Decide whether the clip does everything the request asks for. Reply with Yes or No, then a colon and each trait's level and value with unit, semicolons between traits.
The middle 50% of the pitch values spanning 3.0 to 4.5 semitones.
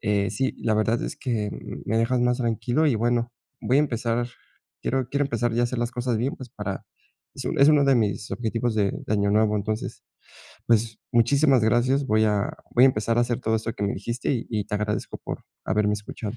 No: narrow, 2.5 semitones